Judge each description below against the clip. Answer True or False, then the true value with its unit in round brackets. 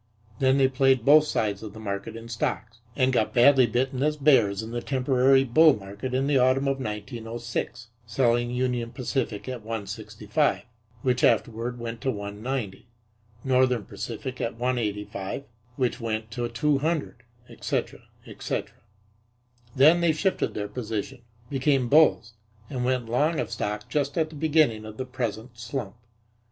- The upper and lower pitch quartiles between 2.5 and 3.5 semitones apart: True (3.2 semitones)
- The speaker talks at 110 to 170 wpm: True (150 wpm)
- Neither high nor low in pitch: False (125 Hz)